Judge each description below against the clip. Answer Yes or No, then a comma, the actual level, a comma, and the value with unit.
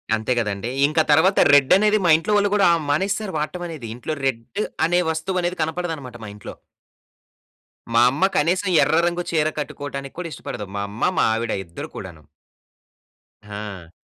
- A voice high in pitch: No, medium, 150 Hz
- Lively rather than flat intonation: Yes, wide, 7.3 semitones